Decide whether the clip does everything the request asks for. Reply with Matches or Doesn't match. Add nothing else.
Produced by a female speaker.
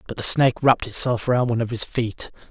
Doesn't match